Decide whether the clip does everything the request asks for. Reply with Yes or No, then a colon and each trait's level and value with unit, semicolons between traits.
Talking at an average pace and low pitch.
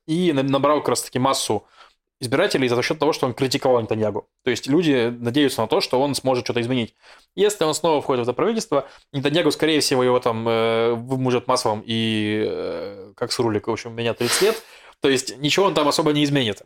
No: fast, 210 wpm; low, 130 Hz